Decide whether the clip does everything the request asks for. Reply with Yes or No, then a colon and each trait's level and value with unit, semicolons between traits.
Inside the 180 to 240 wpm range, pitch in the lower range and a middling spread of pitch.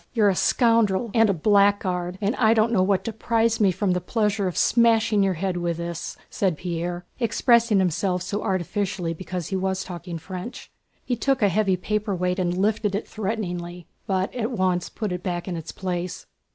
No: average, 185 wpm; high, 190 Hz; average, 3.3 semitones